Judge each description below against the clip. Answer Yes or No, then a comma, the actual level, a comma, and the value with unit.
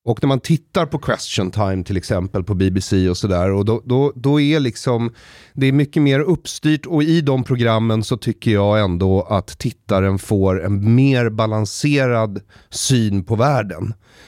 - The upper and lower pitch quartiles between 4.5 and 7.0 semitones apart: Yes, average, 5.2 semitones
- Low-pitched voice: Yes, low, 115 Hz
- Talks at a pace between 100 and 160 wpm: No, average, 175 wpm